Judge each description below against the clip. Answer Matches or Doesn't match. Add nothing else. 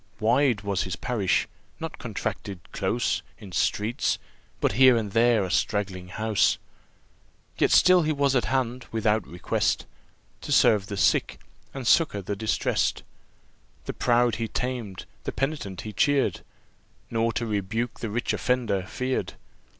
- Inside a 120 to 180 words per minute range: Matches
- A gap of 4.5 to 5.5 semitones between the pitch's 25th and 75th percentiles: Doesn't match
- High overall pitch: Doesn't match